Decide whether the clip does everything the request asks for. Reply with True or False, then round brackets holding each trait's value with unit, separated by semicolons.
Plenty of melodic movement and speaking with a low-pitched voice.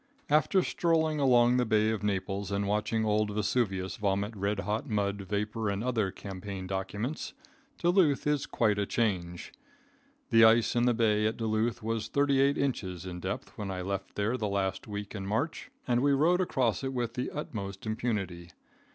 False (3.7 semitones; 110 Hz)